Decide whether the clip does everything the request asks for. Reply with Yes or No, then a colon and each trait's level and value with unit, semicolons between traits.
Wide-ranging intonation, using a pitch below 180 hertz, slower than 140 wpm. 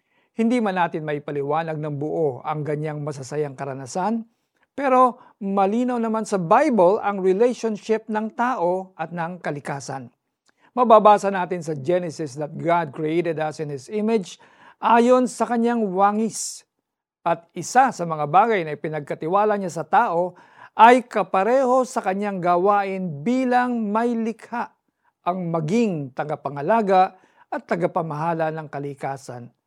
No: wide, 5.9 semitones; medium, 185 Hz; average, 125 wpm